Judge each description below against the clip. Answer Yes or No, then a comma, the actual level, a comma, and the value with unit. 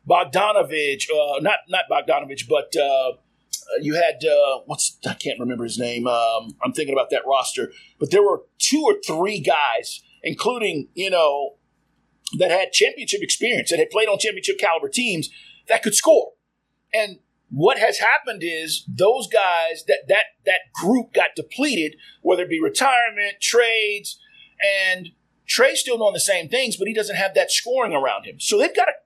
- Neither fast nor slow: Yes, average, 170 wpm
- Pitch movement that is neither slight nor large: No, wide, 7.7 semitones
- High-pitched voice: Yes, high, 205 Hz